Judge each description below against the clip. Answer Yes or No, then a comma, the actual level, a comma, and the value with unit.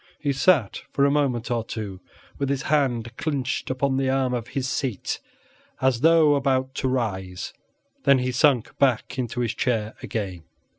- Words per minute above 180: No, average, 165 wpm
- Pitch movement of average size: Yes, average, 3.1 semitones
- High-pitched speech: No, low, 130 Hz